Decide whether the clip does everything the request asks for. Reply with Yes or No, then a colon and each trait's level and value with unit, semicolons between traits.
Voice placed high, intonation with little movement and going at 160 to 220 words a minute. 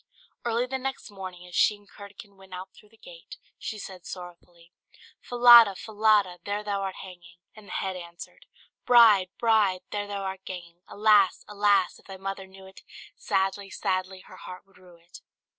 Yes: high, 195 Hz; narrow, 2.3 semitones; average, 175 wpm